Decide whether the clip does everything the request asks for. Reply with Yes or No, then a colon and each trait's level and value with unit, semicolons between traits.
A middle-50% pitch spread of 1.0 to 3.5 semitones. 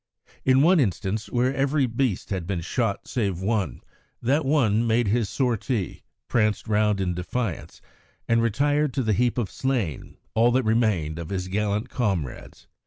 No: average, 4.3 semitones